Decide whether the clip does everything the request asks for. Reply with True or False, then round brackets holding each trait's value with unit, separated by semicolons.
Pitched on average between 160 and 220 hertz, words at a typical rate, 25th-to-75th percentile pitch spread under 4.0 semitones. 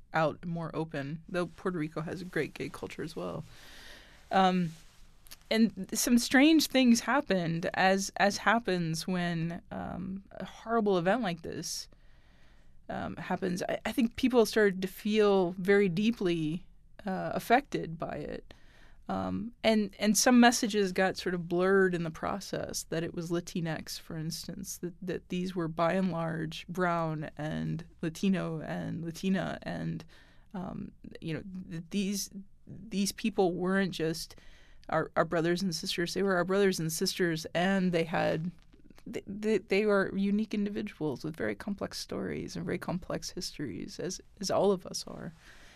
True (185 Hz; 150 wpm; 3.4 semitones)